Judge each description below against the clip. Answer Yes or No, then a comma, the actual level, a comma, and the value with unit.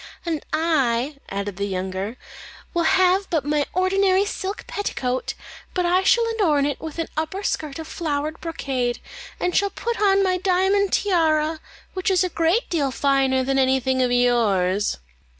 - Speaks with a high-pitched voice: Yes, very high, 315 Hz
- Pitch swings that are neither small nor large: No, wide, 6.1 semitones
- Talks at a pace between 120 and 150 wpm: No, average, 160 wpm